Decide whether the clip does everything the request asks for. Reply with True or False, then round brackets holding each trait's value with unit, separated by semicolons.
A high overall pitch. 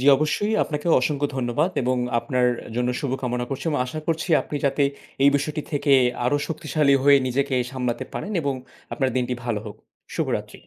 False (140 Hz)